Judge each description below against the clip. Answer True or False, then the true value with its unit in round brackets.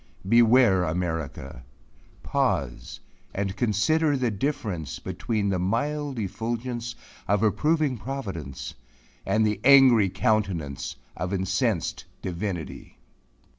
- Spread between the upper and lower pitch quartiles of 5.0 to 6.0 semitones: True (5.5 semitones)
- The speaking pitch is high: False (105 Hz)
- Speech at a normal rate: False (95 wpm)